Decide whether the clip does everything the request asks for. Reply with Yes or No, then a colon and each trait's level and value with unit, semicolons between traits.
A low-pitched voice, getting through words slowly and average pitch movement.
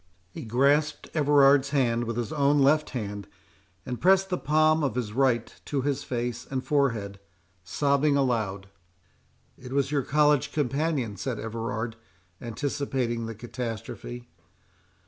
Yes: low, 130 Hz; slow, 130 wpm; average, 3.9 semitones